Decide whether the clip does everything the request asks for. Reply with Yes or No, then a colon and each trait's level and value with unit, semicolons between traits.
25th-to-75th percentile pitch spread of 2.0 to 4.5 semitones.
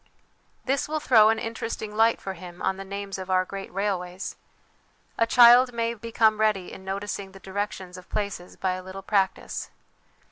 Yes: average, 2.9 semitones